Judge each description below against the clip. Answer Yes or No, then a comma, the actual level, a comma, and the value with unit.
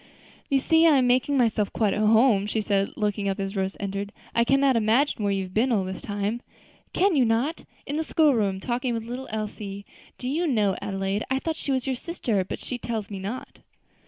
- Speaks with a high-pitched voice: Yes, high, 225 Hz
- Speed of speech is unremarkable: No, fast, 220 wpm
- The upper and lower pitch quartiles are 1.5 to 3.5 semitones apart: No, average, 4.7 semitones